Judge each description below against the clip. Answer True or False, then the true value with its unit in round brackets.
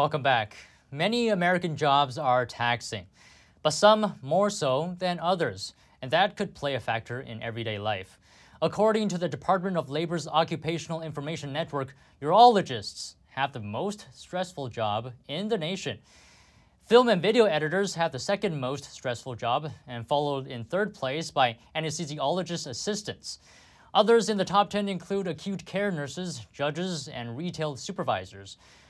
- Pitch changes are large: True (7.2 semitones)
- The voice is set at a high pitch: False (155 Hz)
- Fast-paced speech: False (145 wpm)